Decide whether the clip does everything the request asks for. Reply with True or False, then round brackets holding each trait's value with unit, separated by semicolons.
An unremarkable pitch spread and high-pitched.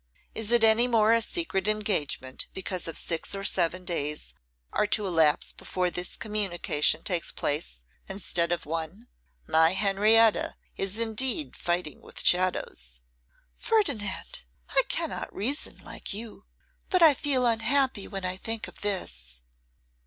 True (4.7 semitones; 195 Hz)